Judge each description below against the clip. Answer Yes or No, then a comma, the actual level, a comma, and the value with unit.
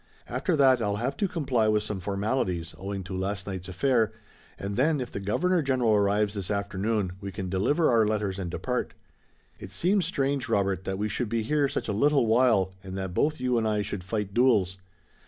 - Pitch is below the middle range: Yes, low, 105 Hz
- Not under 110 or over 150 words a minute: No, fast, 205 wpm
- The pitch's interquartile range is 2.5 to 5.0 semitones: Yes, average, 4.7 semitones